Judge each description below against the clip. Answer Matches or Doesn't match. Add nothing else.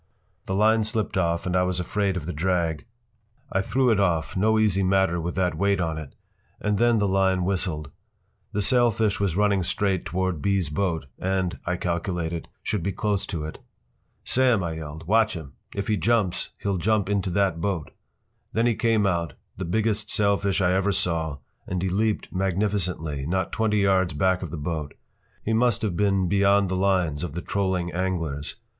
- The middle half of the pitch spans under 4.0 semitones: Matches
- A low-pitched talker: Matches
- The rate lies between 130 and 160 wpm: Doesn't match